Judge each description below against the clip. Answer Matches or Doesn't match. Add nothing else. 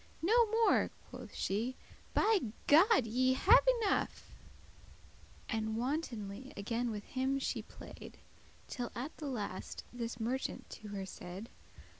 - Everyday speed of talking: Doesn't match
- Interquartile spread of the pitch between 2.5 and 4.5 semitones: Doesn't match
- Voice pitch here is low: Doesn't match